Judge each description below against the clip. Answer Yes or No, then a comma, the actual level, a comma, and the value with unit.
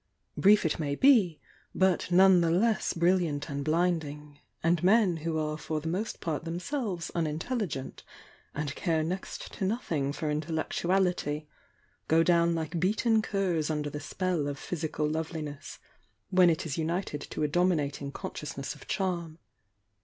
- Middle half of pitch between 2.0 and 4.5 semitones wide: Yes, average, 3.4 semitones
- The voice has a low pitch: No, medium, 165 Hz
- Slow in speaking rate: No, average, 145 wpm